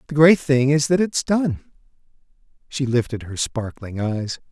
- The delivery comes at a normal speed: Yes, average, 160 wpm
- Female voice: No, male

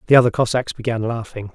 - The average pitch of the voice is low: Yes, low, 115 Hz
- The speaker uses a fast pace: No, average, 195 wpm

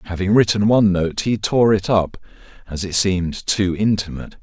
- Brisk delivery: No, average, 175 wpm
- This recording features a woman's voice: No, male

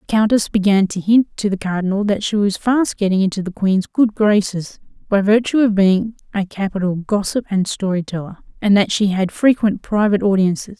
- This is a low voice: No, high, 200 Hz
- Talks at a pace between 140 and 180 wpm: No, average, 195 wpm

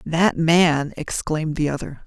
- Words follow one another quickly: No, average, 145 wpm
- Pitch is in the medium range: Yes, medium, 160 Hz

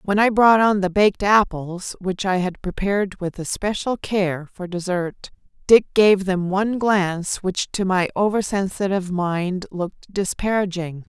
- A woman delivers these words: Yes, female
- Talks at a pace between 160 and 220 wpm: No, average, 150 wpm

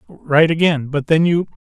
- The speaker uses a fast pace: No, average, 145 wpm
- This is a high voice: No, medium, 155 Hz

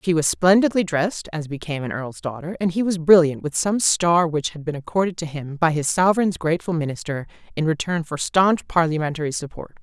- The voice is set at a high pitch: No, medium, 165 Hz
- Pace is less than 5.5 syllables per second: No, 5.8 syllables/s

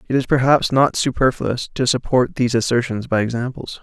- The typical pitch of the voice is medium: No, low, 125 Hz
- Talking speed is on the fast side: No, average, 175 wpm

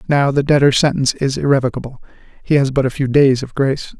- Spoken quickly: Yes, fast, 210 wpm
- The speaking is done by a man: Yes, male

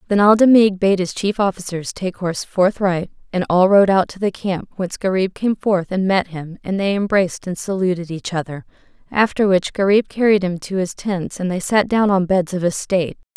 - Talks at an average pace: No, fast, 210 wpm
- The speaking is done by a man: No, female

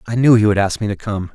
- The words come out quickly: Yes, fast, 360 wpm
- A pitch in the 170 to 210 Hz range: No, low, 105 Hz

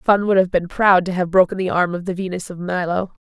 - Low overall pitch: No, medium, 180 Hz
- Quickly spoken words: Yes, fast, 280 wpm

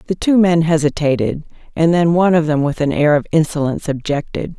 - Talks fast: No, average, 195 wpm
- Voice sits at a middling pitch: Yes, medium, 160 Hz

